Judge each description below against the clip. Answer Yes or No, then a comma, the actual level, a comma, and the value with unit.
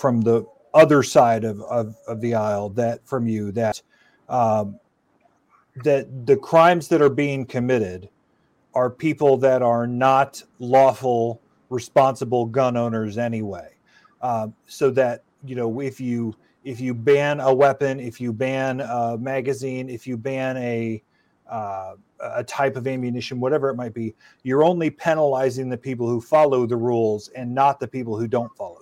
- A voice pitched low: Yes, low, 125 Hz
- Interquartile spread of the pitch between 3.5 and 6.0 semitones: No, narrow, 2.5 semitones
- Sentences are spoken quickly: No, average, 160 wpm